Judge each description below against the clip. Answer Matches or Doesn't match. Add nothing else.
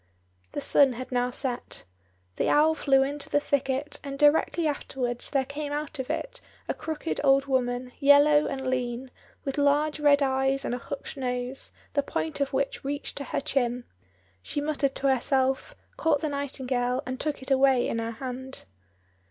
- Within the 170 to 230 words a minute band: Matches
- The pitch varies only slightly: Matches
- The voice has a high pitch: Matches